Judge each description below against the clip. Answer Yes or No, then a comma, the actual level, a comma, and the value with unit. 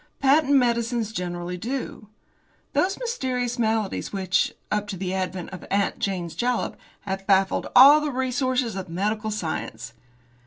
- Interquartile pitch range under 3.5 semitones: No, average, 5.0 semitones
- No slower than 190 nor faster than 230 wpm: No, average, 140 wpm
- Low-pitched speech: No, high, 215 Hz